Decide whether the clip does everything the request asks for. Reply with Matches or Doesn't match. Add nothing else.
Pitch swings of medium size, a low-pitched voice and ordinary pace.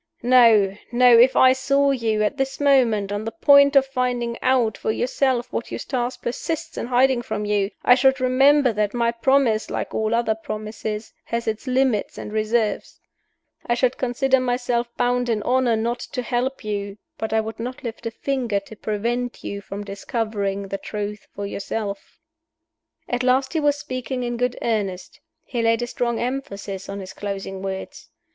Doesn't match